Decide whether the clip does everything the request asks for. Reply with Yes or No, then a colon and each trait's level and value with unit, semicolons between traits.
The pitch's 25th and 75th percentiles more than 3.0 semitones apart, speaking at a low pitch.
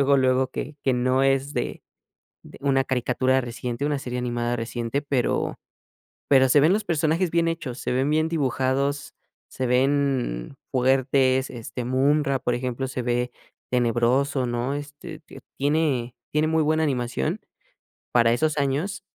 No: average, 2.7 semitones; low, 130 Hz